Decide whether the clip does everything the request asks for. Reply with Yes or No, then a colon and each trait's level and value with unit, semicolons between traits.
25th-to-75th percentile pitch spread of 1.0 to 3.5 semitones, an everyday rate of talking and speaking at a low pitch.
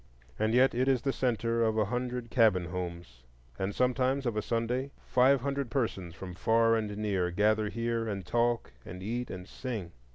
No: average, 4.1 semitones; average, 185 wpm; low, 115 Hz